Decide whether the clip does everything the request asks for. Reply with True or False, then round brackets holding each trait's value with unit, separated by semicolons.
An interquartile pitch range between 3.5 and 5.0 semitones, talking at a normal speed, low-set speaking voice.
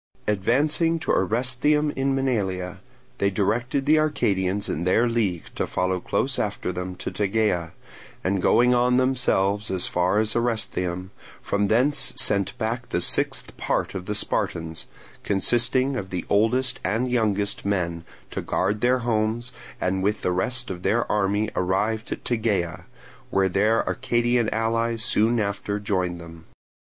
True (4.3 semitones; 145 wpm; 105 Hz)